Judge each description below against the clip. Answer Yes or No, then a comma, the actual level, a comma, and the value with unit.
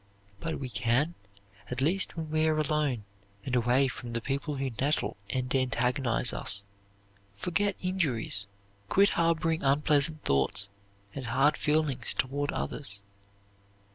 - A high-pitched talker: No, medium, 140 Hz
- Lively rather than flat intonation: No, average, 4.0 semitones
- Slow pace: Yes, slow, 130 wpm